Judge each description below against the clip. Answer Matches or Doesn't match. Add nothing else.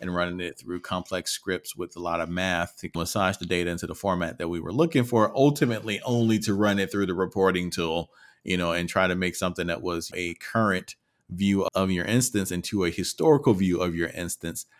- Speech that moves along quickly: Matches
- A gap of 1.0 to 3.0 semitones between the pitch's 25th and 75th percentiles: Matches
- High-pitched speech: Doesn't match